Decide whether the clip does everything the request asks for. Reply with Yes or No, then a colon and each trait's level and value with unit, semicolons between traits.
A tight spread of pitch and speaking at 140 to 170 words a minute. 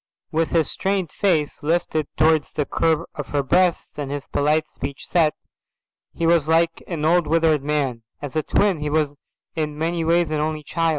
No: narrow, 1.9 semitones; average, 185 wpm